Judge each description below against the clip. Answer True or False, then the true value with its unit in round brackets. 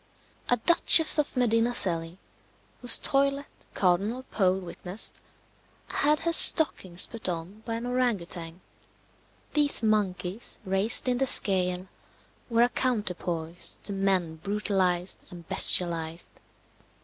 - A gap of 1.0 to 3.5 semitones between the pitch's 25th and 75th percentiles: False (5.5 semitones)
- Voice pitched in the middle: False (195 Hz)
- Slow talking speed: True (115 wpm)